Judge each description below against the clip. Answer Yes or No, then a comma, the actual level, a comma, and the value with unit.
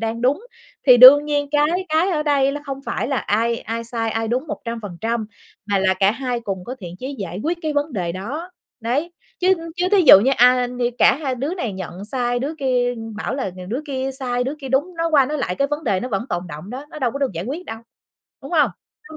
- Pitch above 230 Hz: Yes, very high, 255 Hz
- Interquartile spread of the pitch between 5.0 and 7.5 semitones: No, average, 4.5 semitones